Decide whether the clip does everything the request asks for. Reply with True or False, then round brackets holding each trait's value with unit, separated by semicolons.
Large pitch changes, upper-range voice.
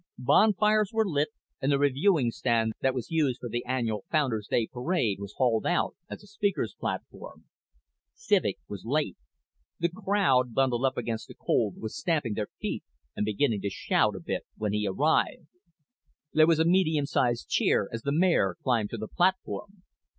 False (7.2 semitones; 130 Hz)